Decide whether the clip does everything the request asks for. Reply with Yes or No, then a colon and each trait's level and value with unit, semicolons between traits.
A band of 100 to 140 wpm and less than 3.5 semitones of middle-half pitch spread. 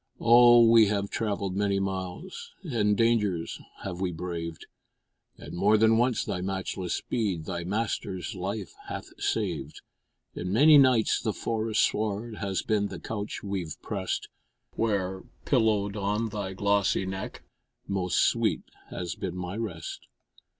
Yes: slow, 135 wpm; average, 3.0 semitones